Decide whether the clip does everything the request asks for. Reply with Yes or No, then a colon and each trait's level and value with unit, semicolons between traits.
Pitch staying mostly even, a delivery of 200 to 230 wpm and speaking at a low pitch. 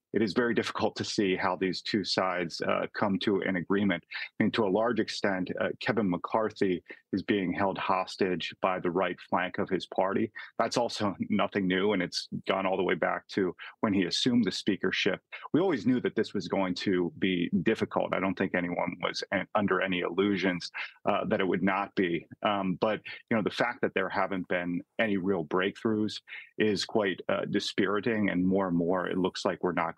Yes: narrow, 1.9 semitones; fast, 205 wpm; very low, 95 Hz